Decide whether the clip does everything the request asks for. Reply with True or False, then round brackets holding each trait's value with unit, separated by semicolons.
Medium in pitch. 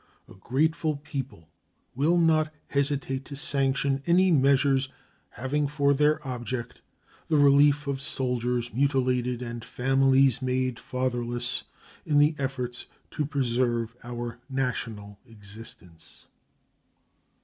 False (130 Hz)